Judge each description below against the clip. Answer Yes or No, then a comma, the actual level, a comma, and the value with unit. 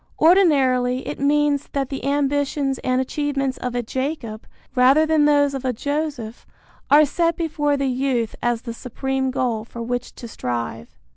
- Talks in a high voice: Yes, very high, 270 Hz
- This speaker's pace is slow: No, average, 160 wpm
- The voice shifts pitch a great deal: No, average, 2.8 semitones